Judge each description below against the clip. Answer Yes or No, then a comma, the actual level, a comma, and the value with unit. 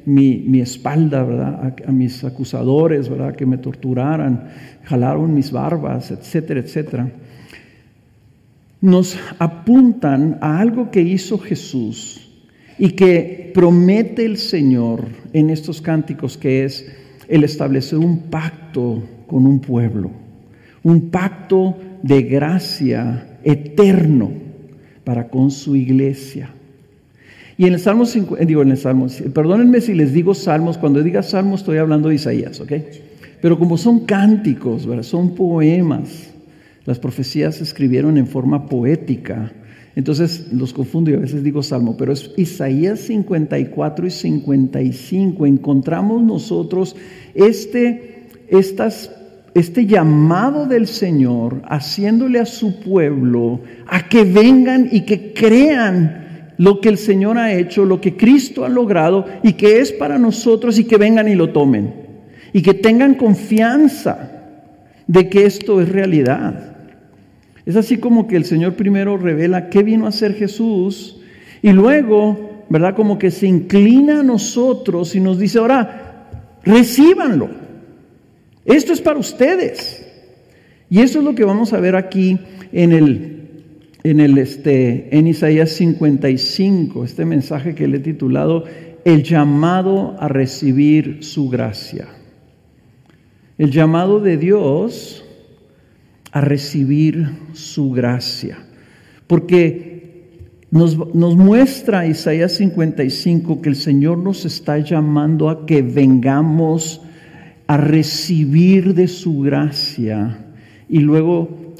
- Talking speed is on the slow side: Yes, slow, 130 wpm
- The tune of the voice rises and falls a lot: Yes, wide, 5.8 semitones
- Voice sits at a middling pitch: Yes, medium, 160 Hz